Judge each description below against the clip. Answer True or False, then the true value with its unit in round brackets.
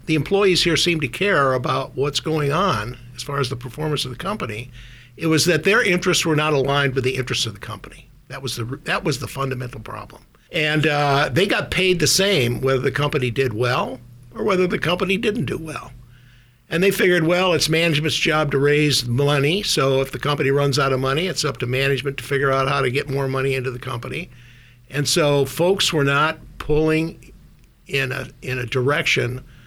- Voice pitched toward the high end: False (140 Hz)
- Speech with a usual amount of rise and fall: True (3.6 semitones)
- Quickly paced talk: True (210 wpm)